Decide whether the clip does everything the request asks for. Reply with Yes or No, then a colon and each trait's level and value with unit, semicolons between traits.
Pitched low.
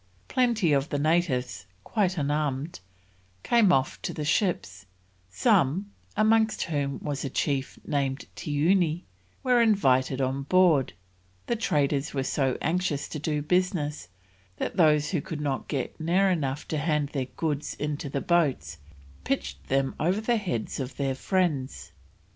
No: medium, 150 Hz